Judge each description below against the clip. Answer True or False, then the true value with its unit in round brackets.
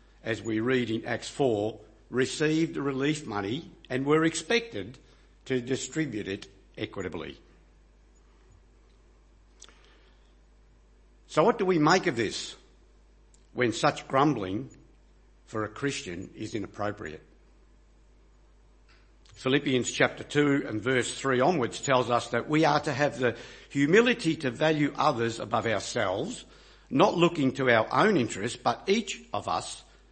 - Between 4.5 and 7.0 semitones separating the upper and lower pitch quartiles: True (5.3 semitones)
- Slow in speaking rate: True (125 wpm)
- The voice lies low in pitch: True (130 Hz)